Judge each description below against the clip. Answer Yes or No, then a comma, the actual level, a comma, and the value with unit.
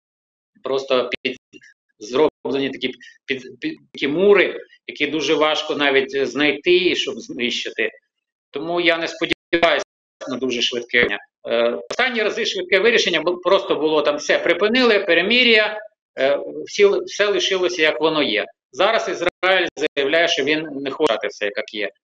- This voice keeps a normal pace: Yes, average, 140 wpm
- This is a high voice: No, medium, 175 Hz